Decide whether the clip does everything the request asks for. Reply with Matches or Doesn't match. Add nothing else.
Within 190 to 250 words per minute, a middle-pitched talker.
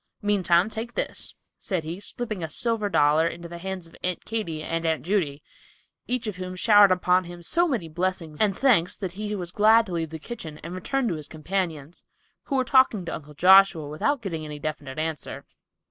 Matches